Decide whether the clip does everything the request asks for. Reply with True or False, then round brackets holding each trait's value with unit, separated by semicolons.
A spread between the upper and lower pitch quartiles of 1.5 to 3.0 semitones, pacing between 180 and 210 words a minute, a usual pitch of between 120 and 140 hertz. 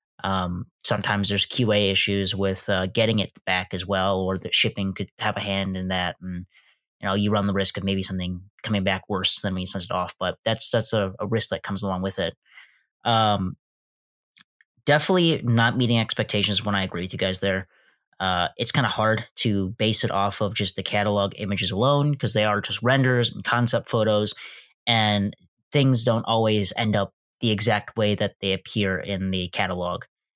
False (2.7 semitones; 200 wpm; 100 Hz)